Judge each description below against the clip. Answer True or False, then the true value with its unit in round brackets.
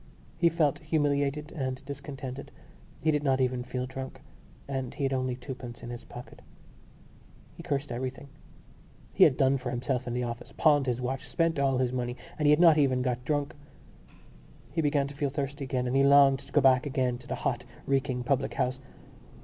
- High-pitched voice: False (135 Hz)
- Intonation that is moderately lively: False (2.1 semitones)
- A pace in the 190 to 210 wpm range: True (195 wpm)